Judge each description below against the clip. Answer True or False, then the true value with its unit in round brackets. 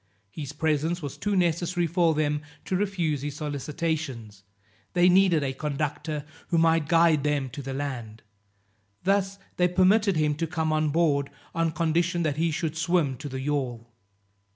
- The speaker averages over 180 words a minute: False (160 wpm)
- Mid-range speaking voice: True (155 Hz)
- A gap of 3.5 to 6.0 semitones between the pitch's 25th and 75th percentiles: False (3.1 semitones)